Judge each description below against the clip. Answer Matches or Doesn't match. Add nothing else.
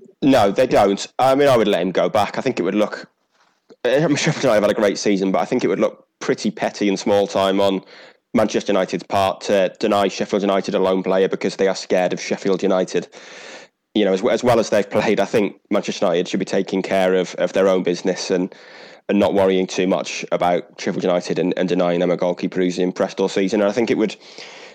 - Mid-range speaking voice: Doesn't match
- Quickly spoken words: Matches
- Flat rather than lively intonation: Matches